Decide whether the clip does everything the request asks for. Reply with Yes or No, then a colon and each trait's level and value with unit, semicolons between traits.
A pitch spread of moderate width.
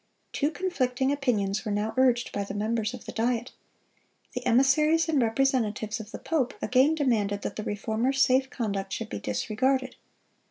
Yes: average, 4.1 semitones